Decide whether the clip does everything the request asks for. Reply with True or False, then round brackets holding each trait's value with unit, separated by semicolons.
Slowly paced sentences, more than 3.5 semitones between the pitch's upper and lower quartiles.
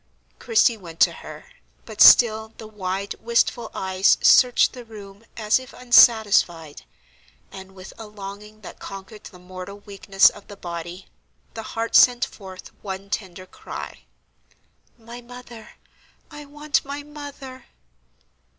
True (130 wpm; 4.0 semitones)